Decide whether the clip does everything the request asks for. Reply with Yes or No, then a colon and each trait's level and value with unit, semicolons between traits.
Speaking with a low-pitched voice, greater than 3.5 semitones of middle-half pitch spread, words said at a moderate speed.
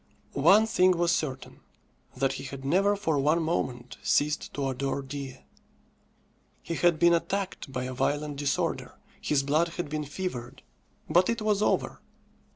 No: medium, 150 Hz; average, 4.3 semitones; average, 155 wpm